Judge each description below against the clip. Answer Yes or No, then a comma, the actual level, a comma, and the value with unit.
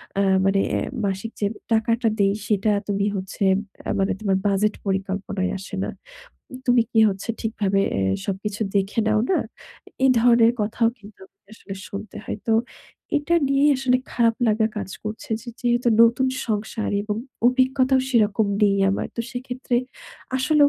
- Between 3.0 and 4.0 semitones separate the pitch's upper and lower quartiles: Yes, average, 3.6 semitones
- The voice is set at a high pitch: Yes, high, 215 Hz